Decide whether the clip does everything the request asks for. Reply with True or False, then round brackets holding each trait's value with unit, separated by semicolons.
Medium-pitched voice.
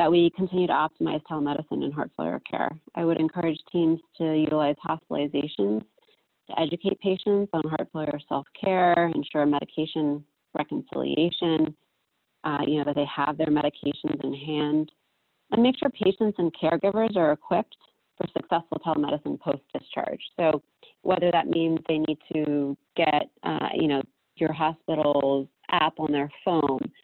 True (155 Hz)